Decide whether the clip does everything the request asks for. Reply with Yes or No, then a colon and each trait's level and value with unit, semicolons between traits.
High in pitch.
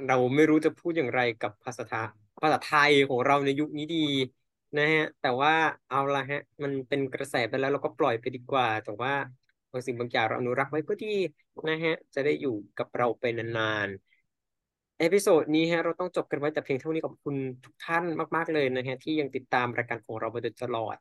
No: medium, 140 Hz